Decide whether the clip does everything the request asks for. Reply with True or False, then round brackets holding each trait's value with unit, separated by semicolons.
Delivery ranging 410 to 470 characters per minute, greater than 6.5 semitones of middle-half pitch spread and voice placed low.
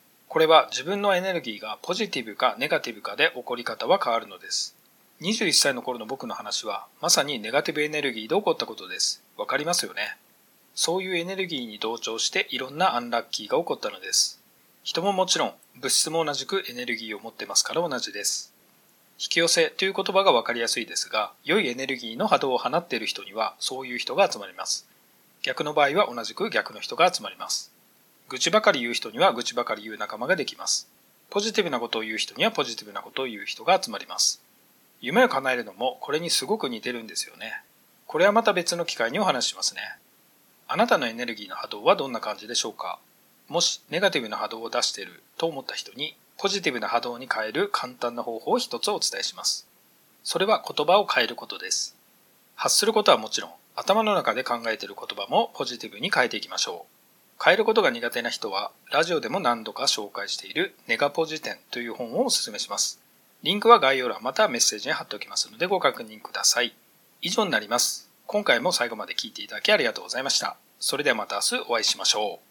False (445 characters per minute; 8.1 semitones; 160 Hz)